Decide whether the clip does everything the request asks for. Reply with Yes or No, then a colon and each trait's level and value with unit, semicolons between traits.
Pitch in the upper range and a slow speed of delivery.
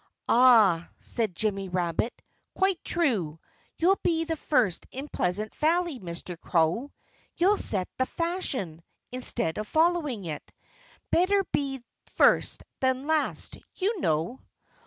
Yes: very high, 255 Hz; slow, 120 wpm